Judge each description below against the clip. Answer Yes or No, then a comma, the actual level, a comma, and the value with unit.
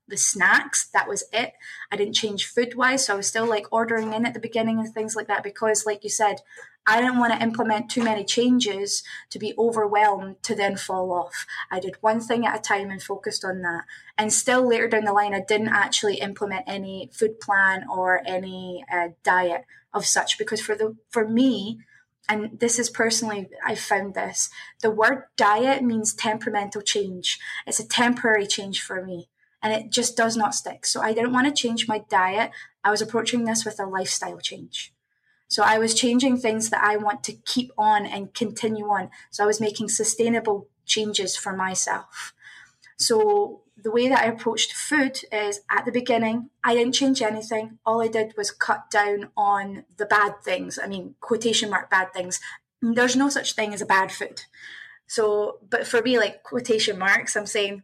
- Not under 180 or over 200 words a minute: Yes, average, 195 wpm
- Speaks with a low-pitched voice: No, high, 215 Hz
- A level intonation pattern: Yes, narrow, 2.2 semitones